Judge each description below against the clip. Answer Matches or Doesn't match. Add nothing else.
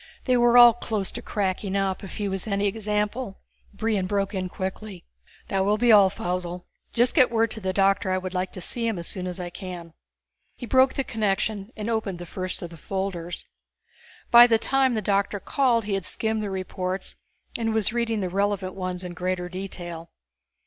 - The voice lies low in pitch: Doesn't match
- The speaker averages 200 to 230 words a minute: Matches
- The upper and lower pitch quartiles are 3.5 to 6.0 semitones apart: Doesn't match